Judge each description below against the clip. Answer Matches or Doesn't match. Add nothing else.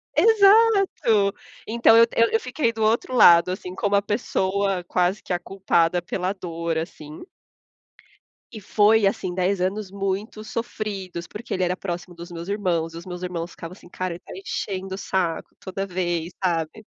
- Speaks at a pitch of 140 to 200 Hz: Matches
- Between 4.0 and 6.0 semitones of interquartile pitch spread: Doesn't match